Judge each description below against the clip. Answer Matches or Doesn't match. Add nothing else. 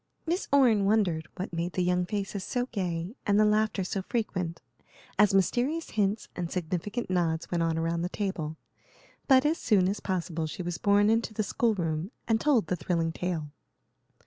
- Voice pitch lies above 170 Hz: Matches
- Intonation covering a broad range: Doesn't match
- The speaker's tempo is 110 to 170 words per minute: Doesn't match